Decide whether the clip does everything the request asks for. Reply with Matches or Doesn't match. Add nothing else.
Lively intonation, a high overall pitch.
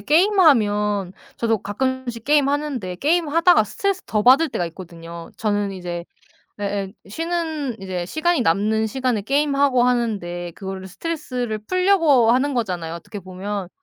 Matches